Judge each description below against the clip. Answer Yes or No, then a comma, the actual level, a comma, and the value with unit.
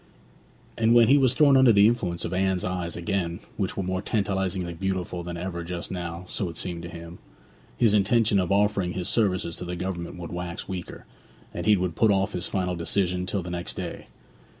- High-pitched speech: No, very low, 90 Hz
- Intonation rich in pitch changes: No, narrow, 2.5 semitones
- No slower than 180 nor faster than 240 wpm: Yes, average, 200 wpm